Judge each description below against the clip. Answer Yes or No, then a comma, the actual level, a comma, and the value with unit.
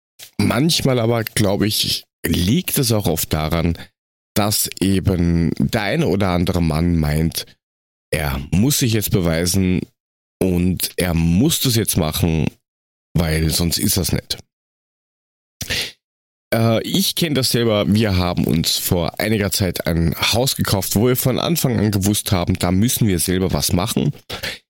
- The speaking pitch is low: Yes, very low, 95 Hz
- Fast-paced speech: No, average, 145 wpm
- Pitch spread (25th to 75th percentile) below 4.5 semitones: No, average, 5.1 semitones